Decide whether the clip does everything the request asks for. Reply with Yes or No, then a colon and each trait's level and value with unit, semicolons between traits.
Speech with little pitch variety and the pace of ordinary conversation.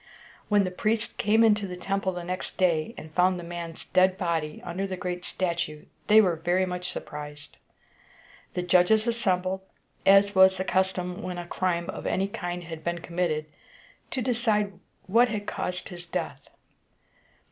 Yes: narrow, 2.3 semitones; average, 165 wpm